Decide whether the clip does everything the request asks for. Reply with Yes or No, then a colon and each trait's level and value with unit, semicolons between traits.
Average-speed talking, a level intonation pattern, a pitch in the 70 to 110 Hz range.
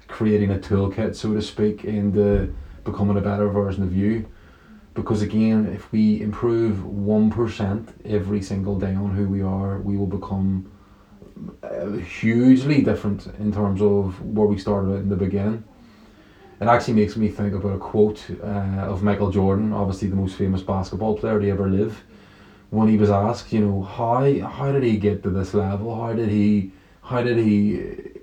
Yes: average, 175 wpm; narrow, 1.6 semitones; low, 105 Hz